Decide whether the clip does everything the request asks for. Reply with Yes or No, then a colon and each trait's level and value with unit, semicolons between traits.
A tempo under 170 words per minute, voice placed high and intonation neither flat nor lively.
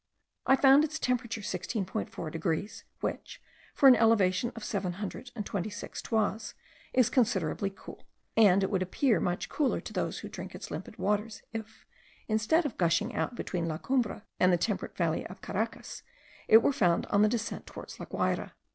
No: average, 180 wpm; high, 210 Hz; average, 4.2 semitones